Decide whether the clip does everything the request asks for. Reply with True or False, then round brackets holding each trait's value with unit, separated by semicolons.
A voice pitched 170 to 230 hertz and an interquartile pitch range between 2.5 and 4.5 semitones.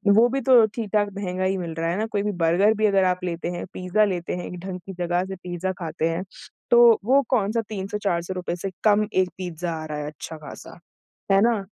True (190 Hz; 3.3 semitones)